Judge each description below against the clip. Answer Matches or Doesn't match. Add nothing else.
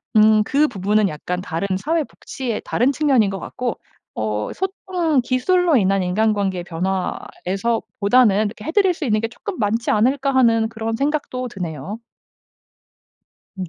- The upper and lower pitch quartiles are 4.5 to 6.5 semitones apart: Matches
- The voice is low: Doesn't match